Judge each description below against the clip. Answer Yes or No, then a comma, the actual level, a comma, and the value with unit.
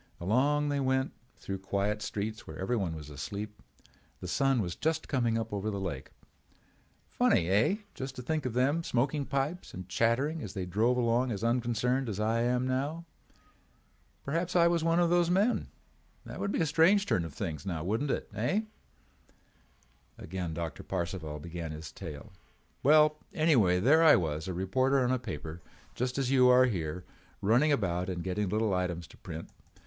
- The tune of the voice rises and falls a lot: Yes, wide, 7.2 semitones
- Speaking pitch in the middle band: No, low, 115 Hz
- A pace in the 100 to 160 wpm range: No, average, 175 wpm